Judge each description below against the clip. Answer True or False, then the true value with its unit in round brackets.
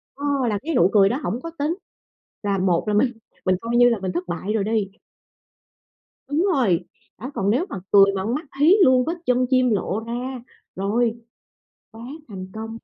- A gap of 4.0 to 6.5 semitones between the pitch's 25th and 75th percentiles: True (4.5 semitones)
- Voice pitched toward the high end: True (225 Hz)